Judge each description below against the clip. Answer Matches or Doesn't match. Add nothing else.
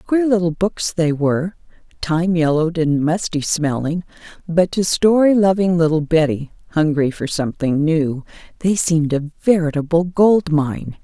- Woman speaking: Matches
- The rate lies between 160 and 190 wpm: Doesn't match